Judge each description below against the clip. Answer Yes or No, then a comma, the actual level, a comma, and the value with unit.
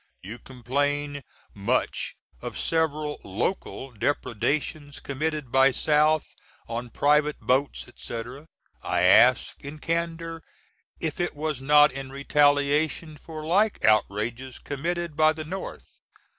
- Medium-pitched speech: Yes, medium, 145 Hz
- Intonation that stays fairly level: No, average, 3.0 semitones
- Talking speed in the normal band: No, slow, 115 wpm